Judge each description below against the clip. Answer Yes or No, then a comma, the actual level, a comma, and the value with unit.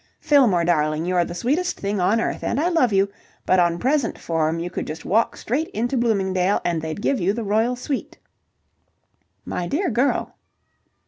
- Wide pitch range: Yes, wide, 6.3 semitones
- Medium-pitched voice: No, high, 205 Hz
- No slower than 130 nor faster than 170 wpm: No, average, 180 wpm